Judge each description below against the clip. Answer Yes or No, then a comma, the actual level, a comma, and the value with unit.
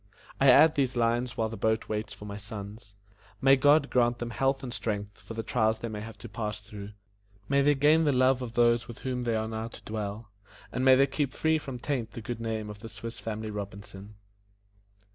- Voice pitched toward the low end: Yes, low, 115 Hz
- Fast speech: Yes, fast, 220 wpm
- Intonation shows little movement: No, average, 3.3 semitones